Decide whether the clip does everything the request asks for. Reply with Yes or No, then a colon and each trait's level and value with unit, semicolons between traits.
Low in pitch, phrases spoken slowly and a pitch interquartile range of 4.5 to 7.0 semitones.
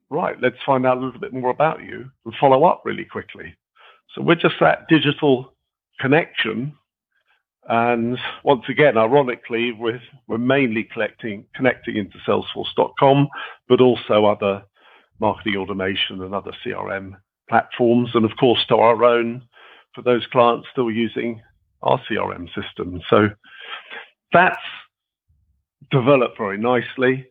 No: low, 120 Hz; slow, 130 wpm; average, 2.8 semitones